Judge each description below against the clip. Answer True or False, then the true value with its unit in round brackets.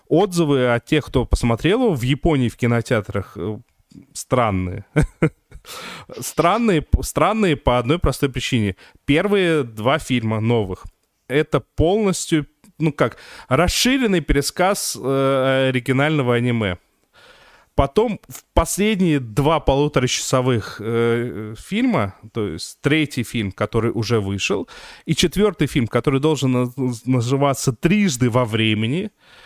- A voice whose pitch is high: False (135 Hz)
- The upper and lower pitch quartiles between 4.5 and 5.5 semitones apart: True (5.2 semitones)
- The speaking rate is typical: False (100 wpm)